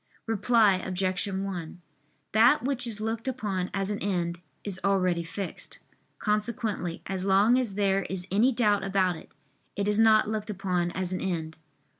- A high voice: Yes, high, 195 Hz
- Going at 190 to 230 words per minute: No, average, 160 wpm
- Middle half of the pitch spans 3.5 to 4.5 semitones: No, narrow, 2.6 semitones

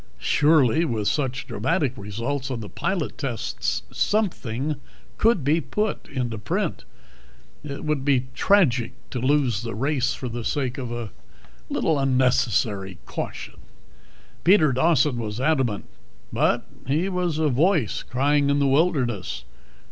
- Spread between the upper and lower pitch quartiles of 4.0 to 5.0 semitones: Yes, average, 4.3 semitones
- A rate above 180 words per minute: No, slow, 135 wpm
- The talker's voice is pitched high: No, low, 135 Hz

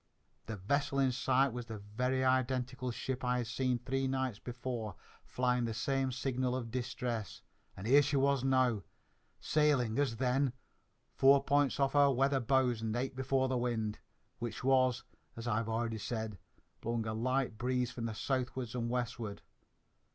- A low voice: Yes, low, 125 Hz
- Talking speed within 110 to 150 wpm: No, average, 165 wpm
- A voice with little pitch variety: Yes, narrow, 2.3 semitones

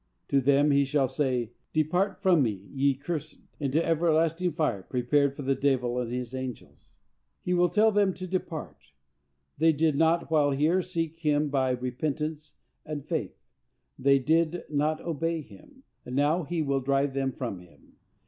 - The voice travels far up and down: No, average, 3.5 semitones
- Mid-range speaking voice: Yes, medium, 145 Hz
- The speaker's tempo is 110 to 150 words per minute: No, average, 165 wpm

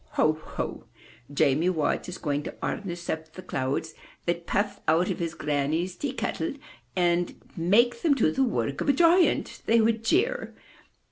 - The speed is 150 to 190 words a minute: Yes, average, 175 wpm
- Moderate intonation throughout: No, wide, 6.2 semitones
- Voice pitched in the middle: Yes, medium, 175 Hz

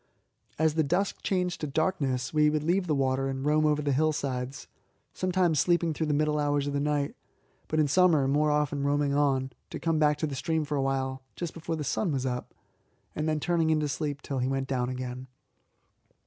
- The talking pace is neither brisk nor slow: No, fast, 215 wpm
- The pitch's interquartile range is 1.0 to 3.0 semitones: Yes, average, 2.7 semitones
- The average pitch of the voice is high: No, medium, 150 Hz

